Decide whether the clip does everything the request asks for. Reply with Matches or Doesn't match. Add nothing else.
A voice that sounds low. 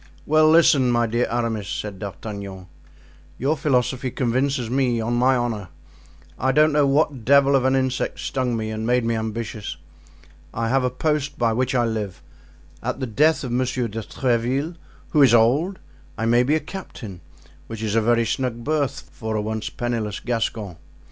Matches